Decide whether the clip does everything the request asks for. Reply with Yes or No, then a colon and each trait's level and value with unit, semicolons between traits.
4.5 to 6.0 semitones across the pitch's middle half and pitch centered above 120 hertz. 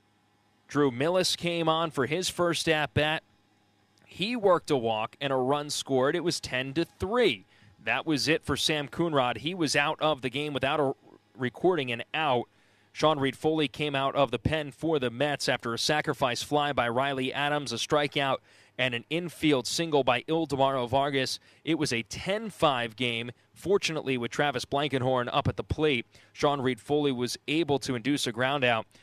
No: average, 4.0 semitones; medium, 140 Hz